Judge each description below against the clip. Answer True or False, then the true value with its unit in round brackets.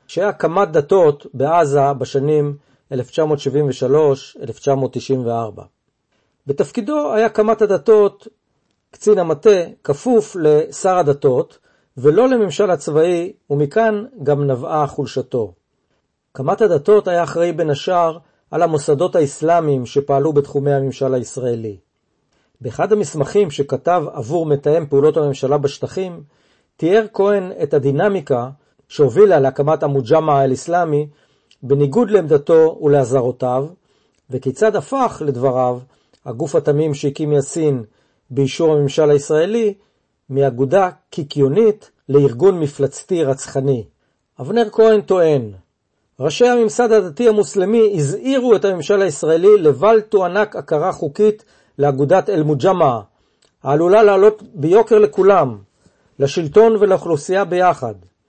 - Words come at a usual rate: False (95 wpm)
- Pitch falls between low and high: True (155 Hz)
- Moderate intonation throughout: False (6.8 semitones)